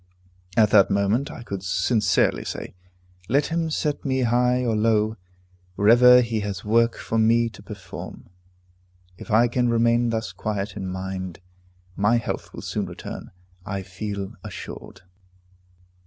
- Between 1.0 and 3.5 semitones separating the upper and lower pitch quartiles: Yes, average, 3.2 semitones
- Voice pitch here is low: Yes, low, 110 Hz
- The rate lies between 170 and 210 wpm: No, average, 140 wpm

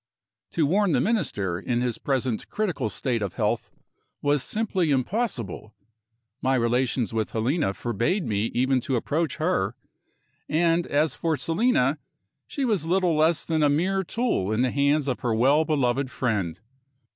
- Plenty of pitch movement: Yes, wide, 5.7 semitones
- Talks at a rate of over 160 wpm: No, average, 155 wpm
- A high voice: No, medium, 140 Hz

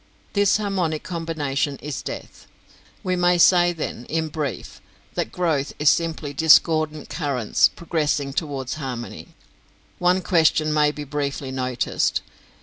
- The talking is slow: Yes, slow, 125 wpm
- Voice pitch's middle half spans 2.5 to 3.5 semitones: Yes, average, 3.1 semitones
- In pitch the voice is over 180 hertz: No, medium, 155 Hz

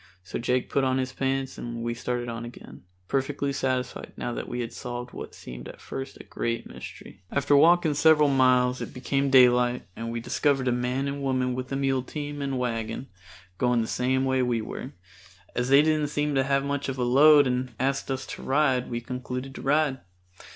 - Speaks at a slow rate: No, fast, 205 wpm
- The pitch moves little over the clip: Yes, narrow, 2.1 semitones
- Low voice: Yes, low, 130 Hz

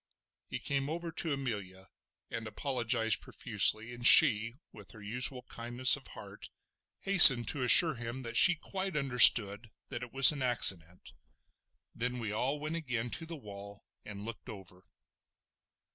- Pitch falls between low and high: No, low, 120 Hz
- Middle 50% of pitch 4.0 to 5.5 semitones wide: Yes, average, 4.4 semitones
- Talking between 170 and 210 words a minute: No, average, 150 wpm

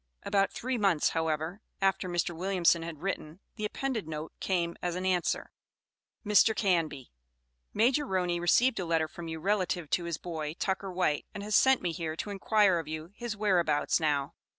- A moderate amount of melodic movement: Yes, average, 3.7 semitones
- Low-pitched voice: No, medium, 180 Hz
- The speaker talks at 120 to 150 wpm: No, average, 175 wpm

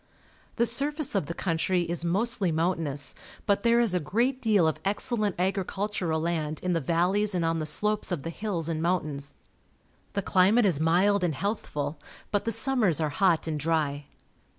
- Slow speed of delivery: No, average, 175 wpm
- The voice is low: No, medium, 180 Hz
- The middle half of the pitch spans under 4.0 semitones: No, average, 4.4 semitones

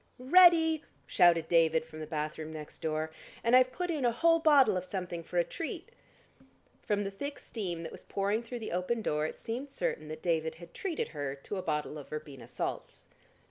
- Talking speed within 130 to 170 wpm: No, average, 200 wpm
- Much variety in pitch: Yes, wide, 8.1 semitones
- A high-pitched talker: No, medium, 180 Hz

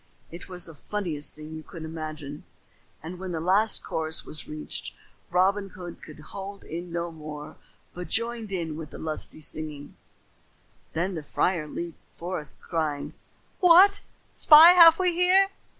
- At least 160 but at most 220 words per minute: No, average, 150 wpm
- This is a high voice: No, medium, 170 Hz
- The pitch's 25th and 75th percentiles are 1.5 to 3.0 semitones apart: No, average, 4.3 semitones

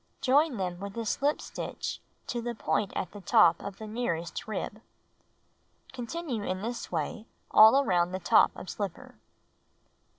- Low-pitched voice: No, high, 215 Hz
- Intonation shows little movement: No, average, 4.5 semitones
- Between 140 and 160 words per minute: Yes, average, 145 wpm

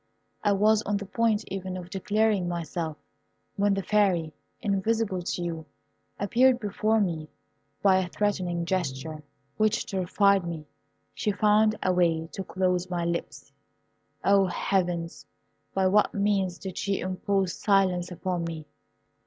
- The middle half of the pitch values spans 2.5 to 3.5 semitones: Yes, average, 2.8 semitones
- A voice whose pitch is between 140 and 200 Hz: Yes, high, 190 Hz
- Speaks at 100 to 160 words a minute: Yes, slow, 135 wpm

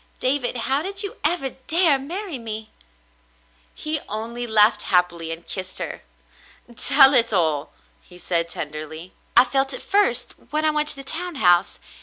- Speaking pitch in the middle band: No, high, 245 Hz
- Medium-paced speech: Yes, average, 160 wpm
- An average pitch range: No, wide, 8.8 semitones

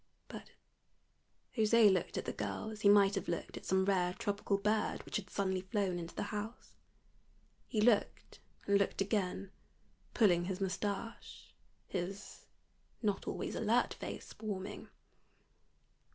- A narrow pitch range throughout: Yes, narrow, 1.9 semitones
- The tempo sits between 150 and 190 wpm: No, slow, 135 wpm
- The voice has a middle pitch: No, high, 200 Hz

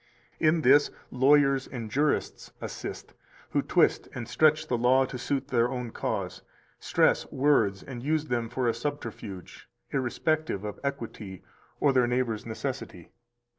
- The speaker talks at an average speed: Yes, average, 150 wpm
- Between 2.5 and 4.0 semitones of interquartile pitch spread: Yes, average, 3.5 semitones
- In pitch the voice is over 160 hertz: No, low, 130 Hz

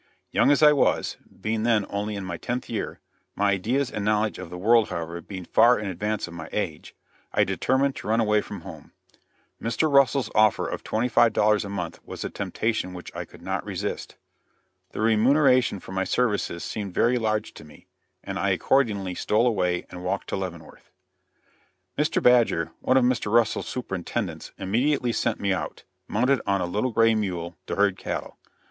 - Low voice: Yes, low, 110 Hz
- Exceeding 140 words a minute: Yes, average, 185 wpm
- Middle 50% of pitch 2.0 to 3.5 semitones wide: No, average, 4.0 semitones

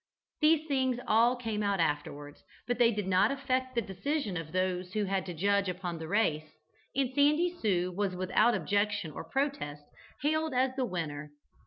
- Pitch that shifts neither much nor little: No, wide, 6.4 semitones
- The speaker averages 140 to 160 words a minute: No, average, 175 wpm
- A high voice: Yes, high, 205 Hz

